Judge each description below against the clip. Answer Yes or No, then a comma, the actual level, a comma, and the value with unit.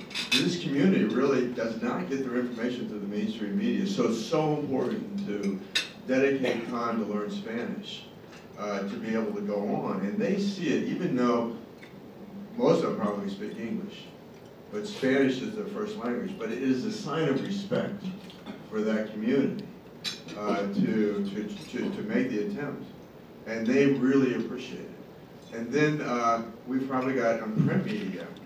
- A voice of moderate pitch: No, low, 130 Hz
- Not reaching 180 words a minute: Yes, average, 165 wpm